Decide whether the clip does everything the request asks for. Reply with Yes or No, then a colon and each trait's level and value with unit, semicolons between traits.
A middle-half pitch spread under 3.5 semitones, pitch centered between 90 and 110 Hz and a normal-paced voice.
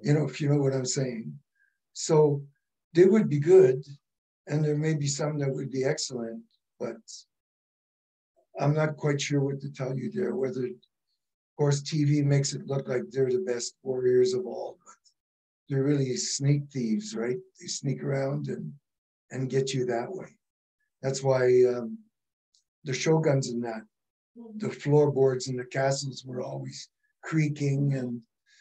No: average, 2.9 semitones; low, 135 Hz; average, 160 wpm